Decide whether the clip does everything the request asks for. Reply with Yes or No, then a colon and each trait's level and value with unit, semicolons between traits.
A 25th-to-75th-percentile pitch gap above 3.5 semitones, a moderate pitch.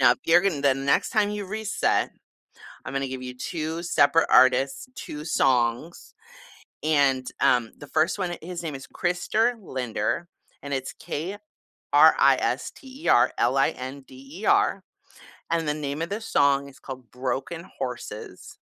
Yes: average, 4.7 semitones; medium, 145 Hz